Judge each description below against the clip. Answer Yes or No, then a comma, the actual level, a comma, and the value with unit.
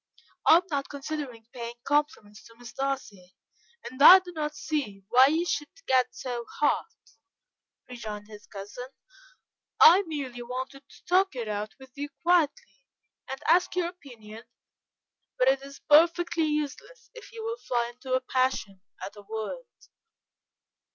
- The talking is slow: No, average, 150 wpm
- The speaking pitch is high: Yes, very high, 270 Hz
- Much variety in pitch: No, average, 4.9 semitones